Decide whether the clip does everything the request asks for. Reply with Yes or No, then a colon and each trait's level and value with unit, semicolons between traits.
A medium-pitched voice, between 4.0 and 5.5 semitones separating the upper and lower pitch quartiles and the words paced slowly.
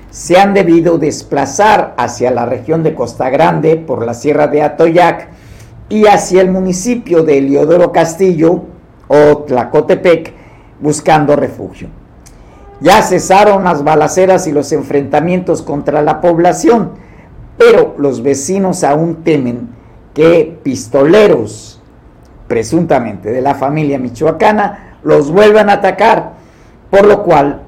Yes: medium, 160 Hz; average, 4.4 semitones; slow, 120 wpm